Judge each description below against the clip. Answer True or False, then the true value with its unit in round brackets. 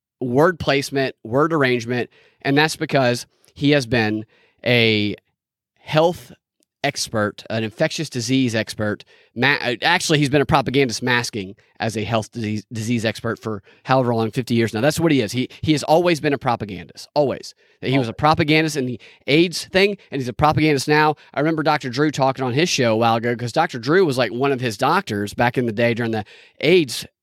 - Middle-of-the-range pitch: False (130 Hz)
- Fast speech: False (190 wpm)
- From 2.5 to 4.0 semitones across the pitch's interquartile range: False (4.7 semitones)